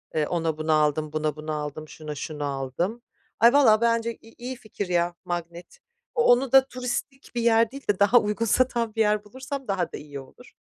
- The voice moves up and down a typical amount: No, wide, 7.3 semitones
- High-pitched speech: Yes, high, 205 Hz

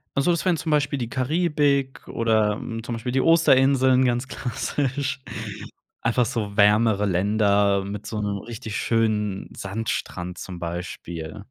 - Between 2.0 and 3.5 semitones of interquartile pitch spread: No, average, 4.6 semitones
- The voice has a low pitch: Yes, low, 115 Hz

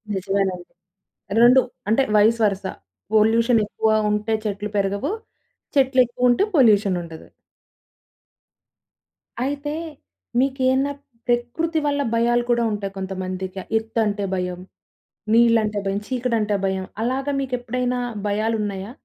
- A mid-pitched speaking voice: No, high, 225 Hz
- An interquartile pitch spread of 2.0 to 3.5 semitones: No, average, 3.9 semitones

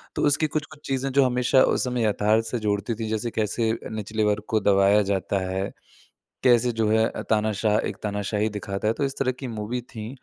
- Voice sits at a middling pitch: No, low, 110 Hz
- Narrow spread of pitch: No, average, 3.0 semitones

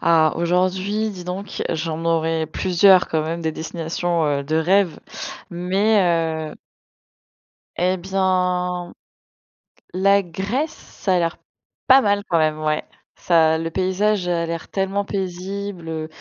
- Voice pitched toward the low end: No, medium, 180 Hz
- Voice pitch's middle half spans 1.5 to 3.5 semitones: Yes, average, 2.8 semitones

